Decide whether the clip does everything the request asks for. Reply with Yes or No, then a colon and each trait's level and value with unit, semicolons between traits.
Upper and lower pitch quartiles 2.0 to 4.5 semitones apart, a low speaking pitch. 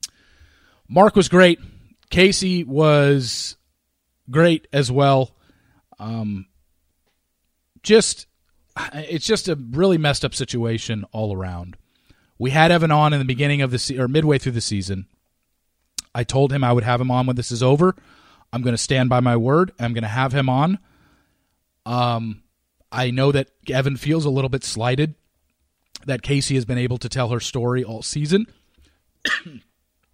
No: average, 5.3 semitones; low, 125 Hz